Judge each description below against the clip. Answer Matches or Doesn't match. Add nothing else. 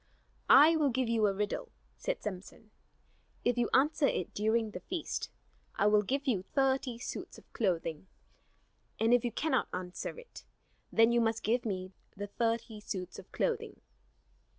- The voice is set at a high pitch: Matches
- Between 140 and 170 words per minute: Matches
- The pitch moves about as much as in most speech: Matches